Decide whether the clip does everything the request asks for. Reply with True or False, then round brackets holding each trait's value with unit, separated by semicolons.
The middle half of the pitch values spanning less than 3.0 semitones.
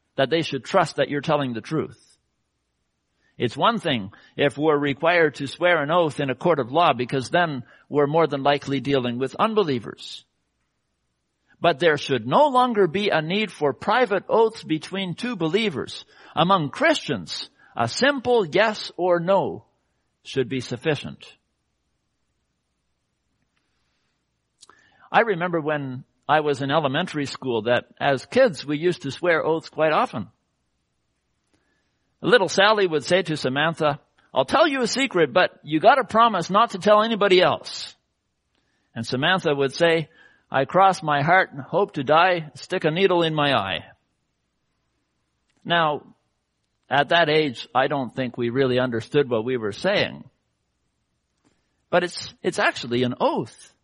False (5.2 semitones)